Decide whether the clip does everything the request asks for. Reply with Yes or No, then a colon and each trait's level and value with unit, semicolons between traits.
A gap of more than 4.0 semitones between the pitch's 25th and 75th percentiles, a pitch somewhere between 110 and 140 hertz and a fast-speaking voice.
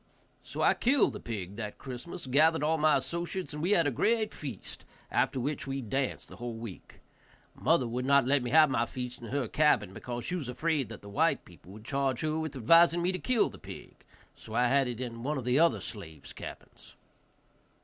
Yes: average, 4.9 semitones; low, 135 Hz; fast, 215 wpm